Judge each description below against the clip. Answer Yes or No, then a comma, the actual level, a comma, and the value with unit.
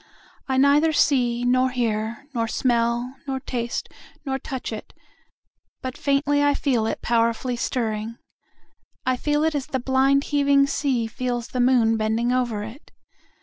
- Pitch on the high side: Yes, very high, 255 Hz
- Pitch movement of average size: Yes, average, 3.0 semitones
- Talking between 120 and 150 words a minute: Yes, average, 145 wpm